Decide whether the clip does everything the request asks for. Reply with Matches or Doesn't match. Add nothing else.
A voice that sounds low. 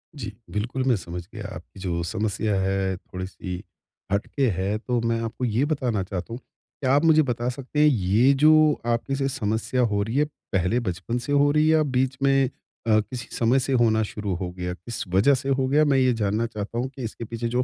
Matches